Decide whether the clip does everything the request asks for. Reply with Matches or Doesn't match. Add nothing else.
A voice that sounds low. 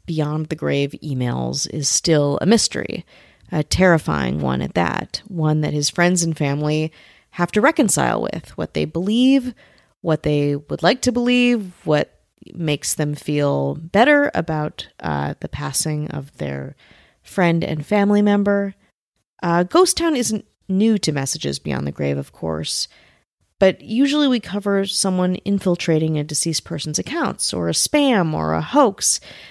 Doesn't match